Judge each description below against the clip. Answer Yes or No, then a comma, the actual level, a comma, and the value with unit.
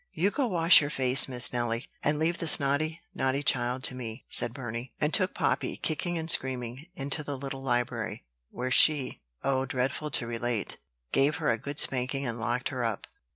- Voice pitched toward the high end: No, low, 135 Hz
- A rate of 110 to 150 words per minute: No, average, 190 wpm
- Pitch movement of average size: Yes, average, 3.4 semitones